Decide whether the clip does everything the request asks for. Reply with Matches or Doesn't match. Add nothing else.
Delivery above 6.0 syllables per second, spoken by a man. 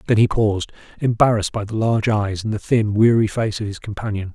Matches